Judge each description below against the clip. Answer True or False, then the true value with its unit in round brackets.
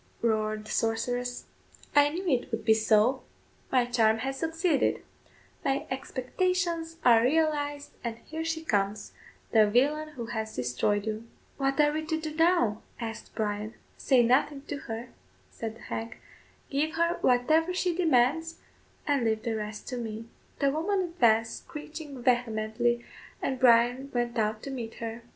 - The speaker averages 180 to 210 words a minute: False (155 wpm)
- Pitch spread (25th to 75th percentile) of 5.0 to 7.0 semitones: True (5.3 semitones)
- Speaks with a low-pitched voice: False (250 Hz)